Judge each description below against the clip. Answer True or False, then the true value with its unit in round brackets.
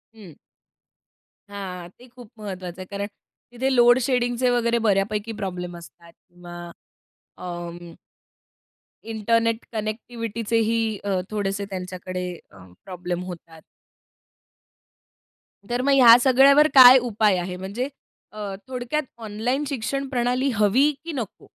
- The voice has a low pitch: False (215 Hz)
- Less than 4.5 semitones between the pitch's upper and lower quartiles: False (5.0 semitones)